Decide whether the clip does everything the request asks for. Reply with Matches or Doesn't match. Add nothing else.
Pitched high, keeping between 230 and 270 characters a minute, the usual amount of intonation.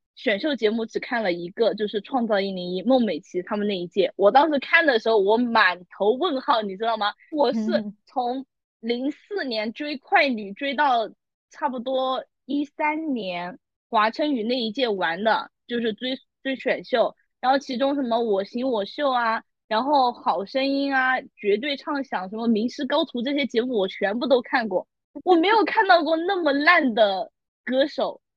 Matches